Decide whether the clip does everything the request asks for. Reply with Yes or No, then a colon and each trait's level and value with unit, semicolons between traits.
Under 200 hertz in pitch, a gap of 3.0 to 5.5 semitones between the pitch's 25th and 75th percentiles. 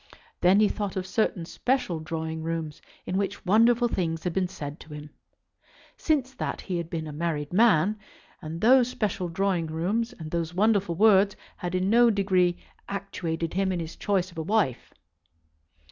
Yes: medium, 185 Hz; average, 4.2 semitones